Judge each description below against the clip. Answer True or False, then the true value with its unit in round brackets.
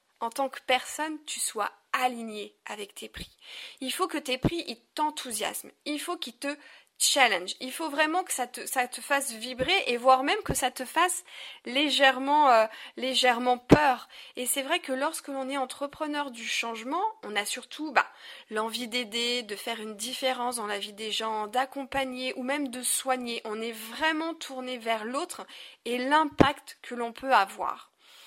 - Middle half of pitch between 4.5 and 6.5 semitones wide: False (3.8 semitones)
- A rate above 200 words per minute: False (180 wpm)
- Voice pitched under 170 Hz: False (255 Hz)